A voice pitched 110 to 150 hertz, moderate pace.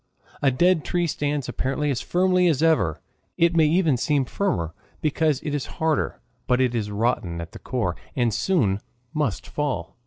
Yes: medium, 140 Hz; average, 175 wpm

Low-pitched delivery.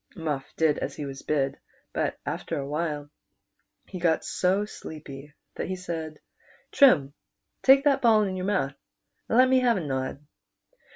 No: medium, 160 Hz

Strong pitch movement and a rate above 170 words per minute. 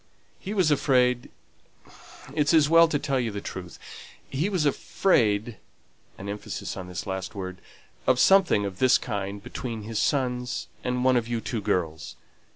No: wide, 5.9 semitones; average, 160 wpm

